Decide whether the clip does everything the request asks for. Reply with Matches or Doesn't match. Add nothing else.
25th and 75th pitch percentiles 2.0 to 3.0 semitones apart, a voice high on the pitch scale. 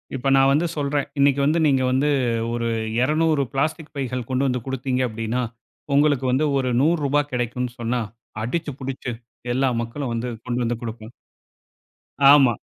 Doesn't match